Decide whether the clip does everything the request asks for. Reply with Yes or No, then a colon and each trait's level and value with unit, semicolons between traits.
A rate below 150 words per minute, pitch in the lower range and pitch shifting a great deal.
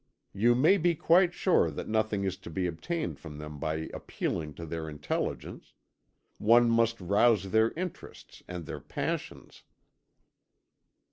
Yes: average, 140 wpm; low, 105 Hz; wide, 6.7 semitones